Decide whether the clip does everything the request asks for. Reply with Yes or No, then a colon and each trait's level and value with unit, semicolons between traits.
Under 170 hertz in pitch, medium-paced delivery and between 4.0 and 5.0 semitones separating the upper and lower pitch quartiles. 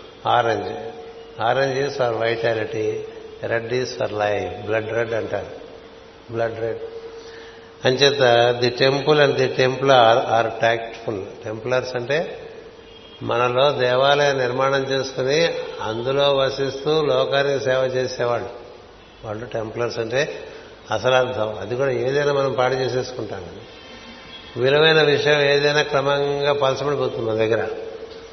No: low, 135 Hz; average, 105 wpm; average, 3.5 semitones